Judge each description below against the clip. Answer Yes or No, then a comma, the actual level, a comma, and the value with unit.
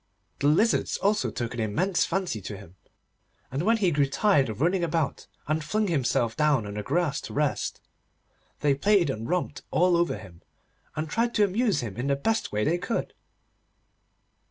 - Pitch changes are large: Yes, wide, 7.4 semitones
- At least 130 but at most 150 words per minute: No, average, 180 wpm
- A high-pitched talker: No, medium, 155 Hz